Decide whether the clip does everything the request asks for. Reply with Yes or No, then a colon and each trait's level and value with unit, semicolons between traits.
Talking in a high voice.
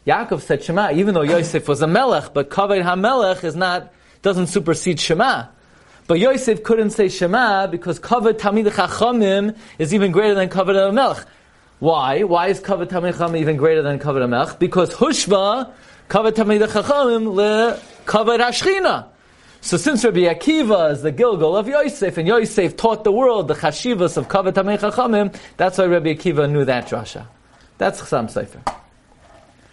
Yes: high, 195 Hz